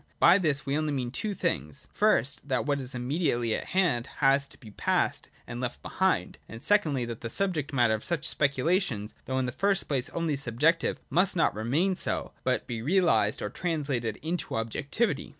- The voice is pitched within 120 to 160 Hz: Yes, medium, 140 Hz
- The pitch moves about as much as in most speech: No, wide, 5.8 semitones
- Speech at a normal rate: Yes, average, 185 wpm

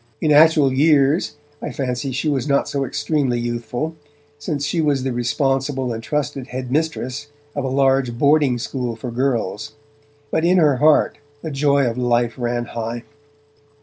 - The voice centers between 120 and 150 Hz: Yes, low, 135 Hz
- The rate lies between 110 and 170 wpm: Yes, average, 155 wpm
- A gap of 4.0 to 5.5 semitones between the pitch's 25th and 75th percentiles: No, average, 3.2 semitones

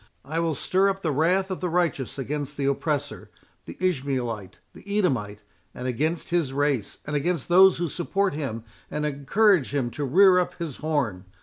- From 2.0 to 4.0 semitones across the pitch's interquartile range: No, average, 4.9 semitones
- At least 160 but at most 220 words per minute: Yes, average, 165 wpm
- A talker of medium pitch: Yes, medium, 150 Hz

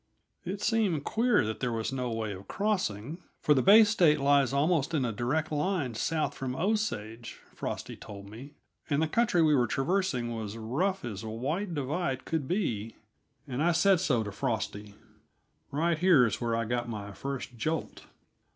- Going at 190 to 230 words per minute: No, average, 175 wpm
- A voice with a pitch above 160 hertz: No, medium, 140 Hz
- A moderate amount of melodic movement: No, wide, 6.9 semitones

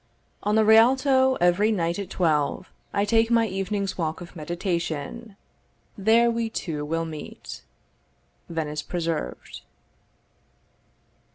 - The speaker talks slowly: Yes, slow, 110 wpm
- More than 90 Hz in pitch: Yes, high, 190 Hz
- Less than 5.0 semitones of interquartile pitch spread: No, average, 5.3 semitones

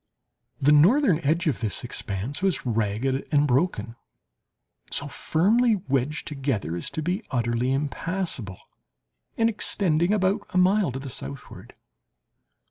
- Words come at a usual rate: No, slow, 130 wpm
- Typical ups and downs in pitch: No, wide, 6.9 semitones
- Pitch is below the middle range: No, medium, 145 Hz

